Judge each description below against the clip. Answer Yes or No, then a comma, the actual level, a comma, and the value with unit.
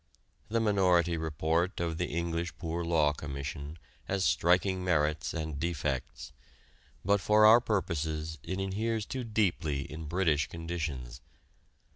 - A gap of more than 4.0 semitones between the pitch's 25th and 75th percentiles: No, average, 3.7 semitones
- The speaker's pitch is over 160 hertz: No, very low, 85 Hz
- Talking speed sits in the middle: No, slow, 125 wpm